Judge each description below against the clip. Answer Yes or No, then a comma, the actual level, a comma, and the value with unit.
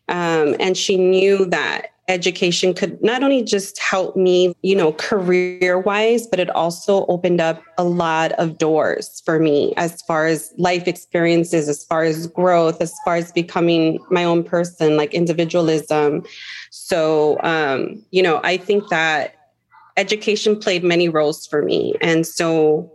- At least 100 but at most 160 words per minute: Yes, average, 155 wpm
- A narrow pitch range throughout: Yes, narrow, 2.3 semitones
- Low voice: No, medium, 175 Hz